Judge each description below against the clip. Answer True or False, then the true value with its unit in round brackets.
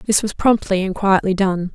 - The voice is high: True (195 Hz)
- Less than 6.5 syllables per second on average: True (5.0 syllables/s)